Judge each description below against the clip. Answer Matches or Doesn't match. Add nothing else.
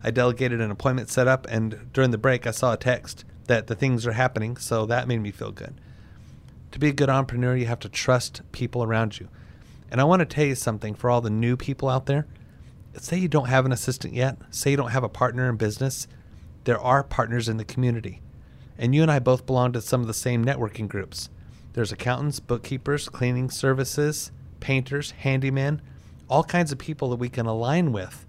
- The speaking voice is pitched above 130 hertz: Doesn't match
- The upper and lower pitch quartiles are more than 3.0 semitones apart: Doesn't match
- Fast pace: Matches